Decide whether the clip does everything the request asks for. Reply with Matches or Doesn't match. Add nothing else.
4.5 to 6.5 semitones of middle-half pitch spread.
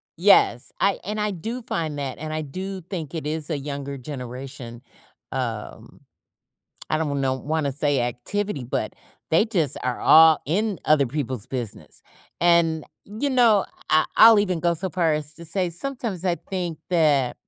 Matches